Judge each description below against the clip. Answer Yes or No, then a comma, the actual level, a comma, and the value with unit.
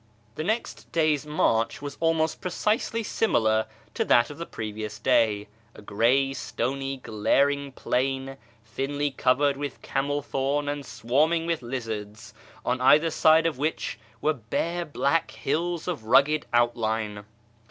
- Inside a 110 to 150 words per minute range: Yes, average, 140 wpm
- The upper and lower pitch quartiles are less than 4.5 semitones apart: No, average, 4.8 semitones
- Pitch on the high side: No, low, 135 Hz